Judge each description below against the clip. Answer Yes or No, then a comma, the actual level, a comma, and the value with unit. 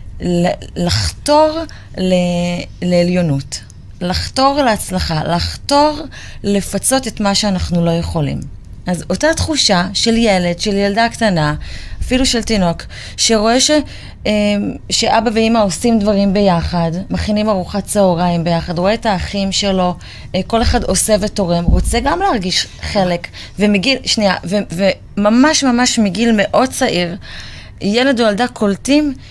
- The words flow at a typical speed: Yes, average, 115 wpm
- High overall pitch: Yes, high, 200 Hz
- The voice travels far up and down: No, average, 4.6 semitones